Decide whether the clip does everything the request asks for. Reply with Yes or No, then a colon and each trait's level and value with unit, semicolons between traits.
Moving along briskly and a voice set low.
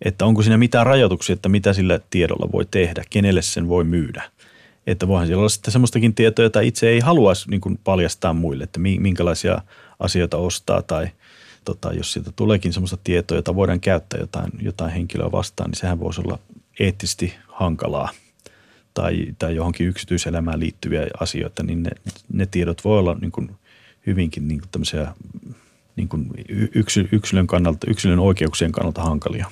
Yes: fast, 160 wpm; very low, 95 Hz